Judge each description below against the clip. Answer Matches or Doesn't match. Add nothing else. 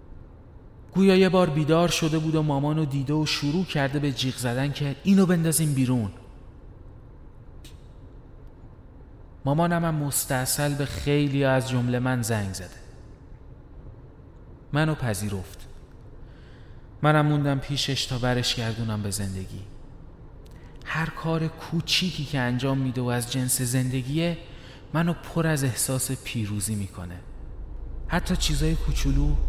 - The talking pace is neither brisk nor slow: Matches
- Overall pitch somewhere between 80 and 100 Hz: Doesn't match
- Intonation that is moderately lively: Doesn't match